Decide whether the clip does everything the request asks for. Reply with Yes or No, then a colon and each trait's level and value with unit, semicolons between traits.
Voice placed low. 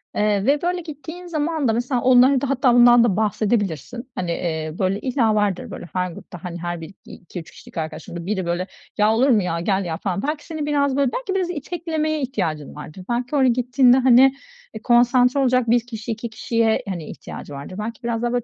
No: high, 235 Hz